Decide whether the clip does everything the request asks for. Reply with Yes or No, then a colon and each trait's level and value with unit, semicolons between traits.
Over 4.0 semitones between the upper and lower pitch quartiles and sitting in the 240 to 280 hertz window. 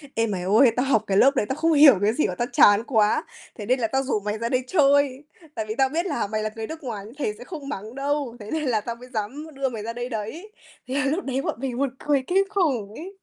Yes: average, 4.5 semitones; very high, 255 Hz